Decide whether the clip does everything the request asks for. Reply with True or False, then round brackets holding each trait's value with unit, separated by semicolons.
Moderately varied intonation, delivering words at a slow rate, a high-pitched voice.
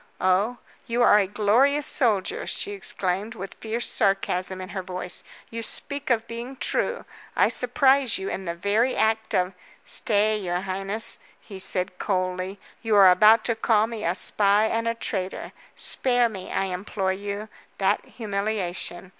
False (3.4 semitones; 165 wpm; 205 Hz)